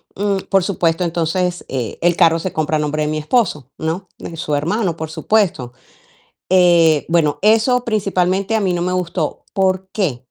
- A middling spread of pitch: Yes, average, 3.4 semitones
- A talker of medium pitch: Yes, medium, 175 Hz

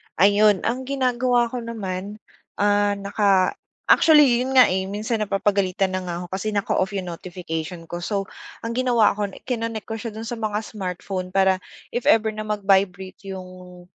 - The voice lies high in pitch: Yes, high, 205 Hz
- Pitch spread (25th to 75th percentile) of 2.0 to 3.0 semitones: No, average, 3.4 semitones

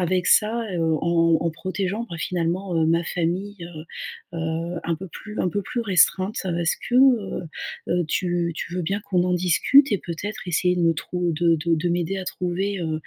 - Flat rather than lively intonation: Yes, narrow, 2.3 semitones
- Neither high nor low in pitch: Yes, medium, 175 Hz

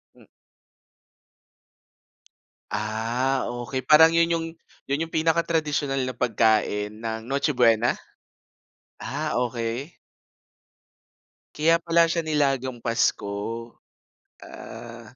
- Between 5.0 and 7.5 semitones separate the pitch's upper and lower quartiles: Yes, average, 5.3 semitones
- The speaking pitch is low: Yes, low, 130 Hz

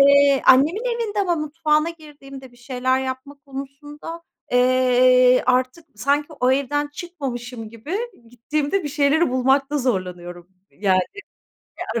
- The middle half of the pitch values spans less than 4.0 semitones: Yes, average, 3.1 semitones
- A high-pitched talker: Yes, very high, 275 Hz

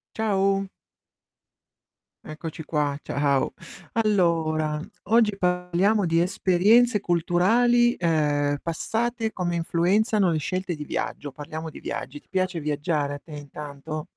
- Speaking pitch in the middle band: Yes, medium, 175 Hz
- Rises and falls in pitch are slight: No, average, 4.6 semitones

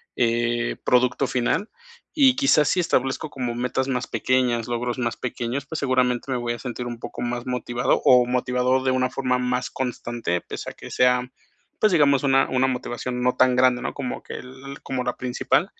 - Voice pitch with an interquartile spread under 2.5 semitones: Yes, narrow, 1.3 semitones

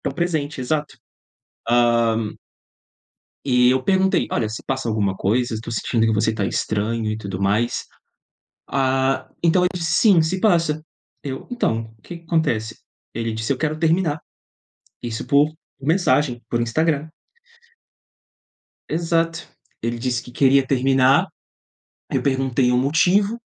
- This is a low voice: Yes, low, 130 Hz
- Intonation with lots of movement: Yes, wide, 5.7 semitones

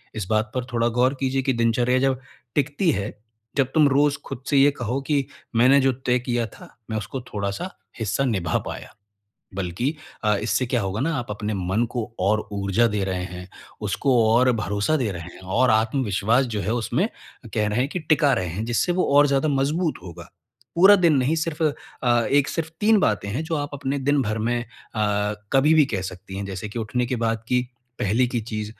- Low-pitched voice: Yes, low, 120 Hz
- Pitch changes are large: No, average, 4.7 semitones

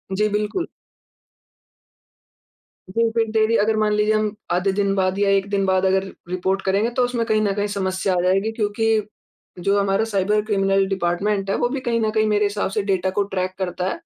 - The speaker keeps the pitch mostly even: Yes, narrow, 2.0 semitones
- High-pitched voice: Yes, high, 205 Hz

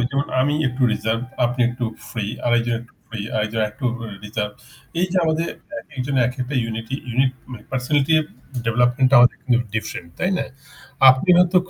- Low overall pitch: Yes, low, 125 Hz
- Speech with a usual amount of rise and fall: Yes, average, 3.1 semitones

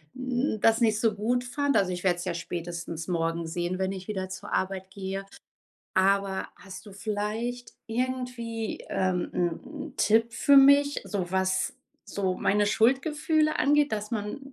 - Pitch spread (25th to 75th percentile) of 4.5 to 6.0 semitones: Yes, average, 4.8 semitones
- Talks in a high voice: Yes, high, 210 Hz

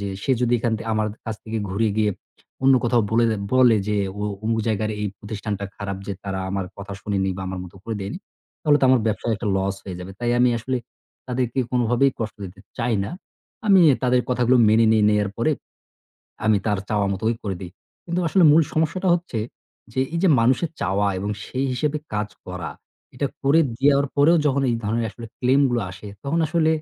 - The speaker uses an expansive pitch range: No, average, 4.2 semitones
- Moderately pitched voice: No, low, 115 Hz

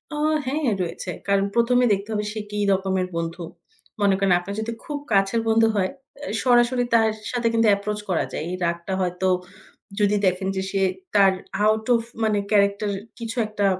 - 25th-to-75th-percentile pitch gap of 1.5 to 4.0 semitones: Yes, average, 3.1 semitones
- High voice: Yes, high, 205 Hz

